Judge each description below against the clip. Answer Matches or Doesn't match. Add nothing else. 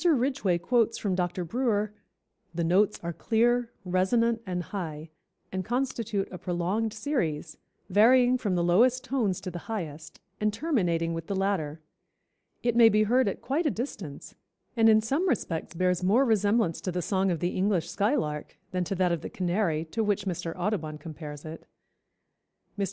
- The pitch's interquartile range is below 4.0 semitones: Doesn't match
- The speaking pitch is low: Doesn't match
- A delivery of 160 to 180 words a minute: Matches